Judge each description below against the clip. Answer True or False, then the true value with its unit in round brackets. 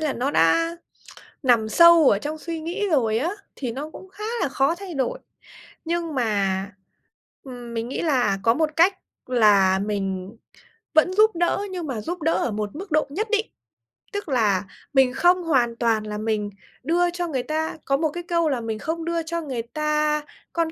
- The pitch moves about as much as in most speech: False (6.8 semitones)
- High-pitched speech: True (295 Hz)